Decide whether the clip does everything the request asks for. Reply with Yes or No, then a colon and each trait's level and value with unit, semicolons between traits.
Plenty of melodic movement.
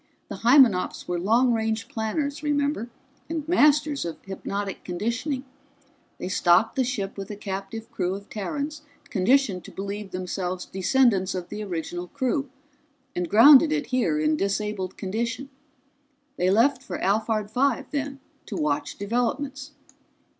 Yes: wide, 6.2 semitones